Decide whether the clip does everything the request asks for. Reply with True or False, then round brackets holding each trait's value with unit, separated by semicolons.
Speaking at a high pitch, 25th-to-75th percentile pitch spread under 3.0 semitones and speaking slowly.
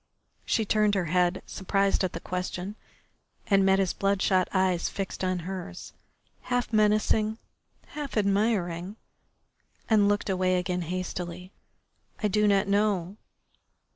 True (195 Hz; 2.4 semitones; 125 wpm)